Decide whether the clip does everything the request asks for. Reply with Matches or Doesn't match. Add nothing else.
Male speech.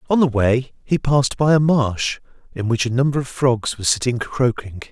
Matches